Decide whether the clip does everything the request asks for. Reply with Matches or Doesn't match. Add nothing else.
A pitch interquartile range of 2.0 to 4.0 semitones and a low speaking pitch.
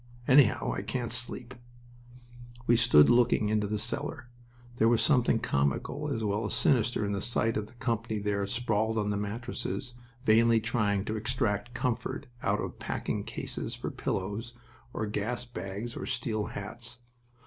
Matches